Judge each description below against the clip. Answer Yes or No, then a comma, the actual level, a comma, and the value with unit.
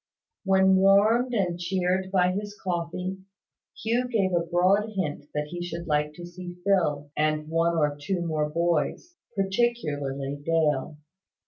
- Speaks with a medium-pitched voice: Yes, medium, 175 Hz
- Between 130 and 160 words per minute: Yes, average, 140 wpm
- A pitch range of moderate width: Yes, average, 4.0 semitones